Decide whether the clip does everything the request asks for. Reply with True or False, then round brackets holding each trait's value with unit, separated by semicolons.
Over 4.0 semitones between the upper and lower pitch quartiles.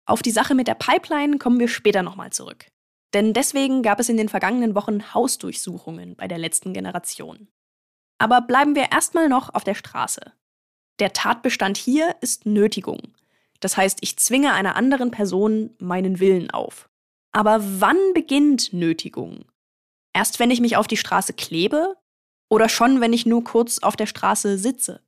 True (4.9 semitones)